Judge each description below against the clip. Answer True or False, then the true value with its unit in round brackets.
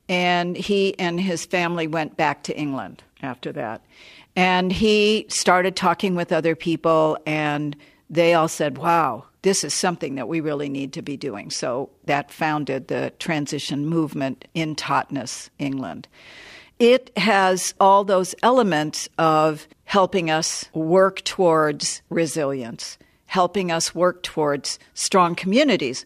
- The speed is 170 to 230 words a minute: False (135 wpm)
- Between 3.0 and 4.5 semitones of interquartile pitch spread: True (3.4 semitones)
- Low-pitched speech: False (165 Hz)